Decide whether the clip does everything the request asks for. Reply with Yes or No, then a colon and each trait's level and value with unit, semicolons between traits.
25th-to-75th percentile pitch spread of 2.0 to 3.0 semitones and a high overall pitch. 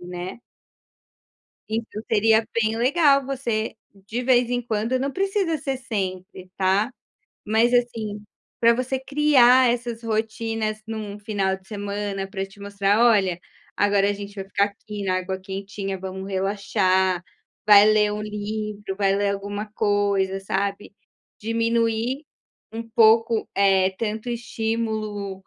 Yes: narrow, 2.6 semitones; high, 210 Hz